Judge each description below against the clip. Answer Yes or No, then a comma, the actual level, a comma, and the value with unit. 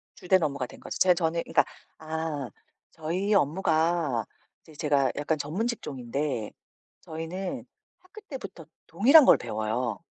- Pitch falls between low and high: Yes, medium, 160 Hz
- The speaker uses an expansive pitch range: No, average, 5.0 semitones